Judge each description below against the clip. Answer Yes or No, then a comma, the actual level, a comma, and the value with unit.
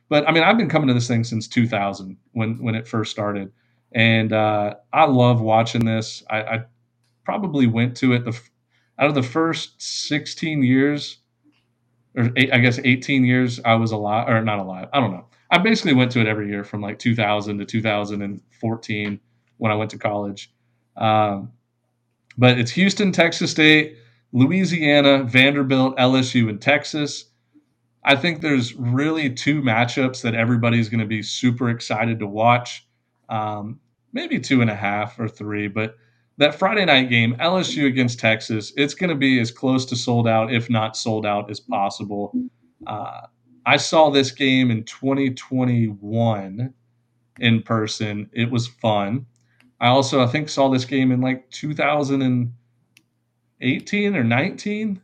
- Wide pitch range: No, average, 3.2 semitones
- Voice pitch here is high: No, low, 120 Hz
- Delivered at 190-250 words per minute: No, average, 160 wpm